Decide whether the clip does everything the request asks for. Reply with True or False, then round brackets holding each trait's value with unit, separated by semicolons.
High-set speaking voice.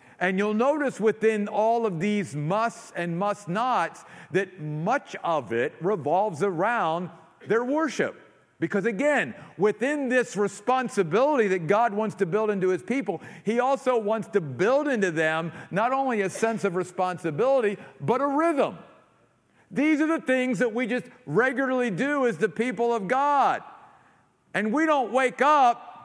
True (220 Hz)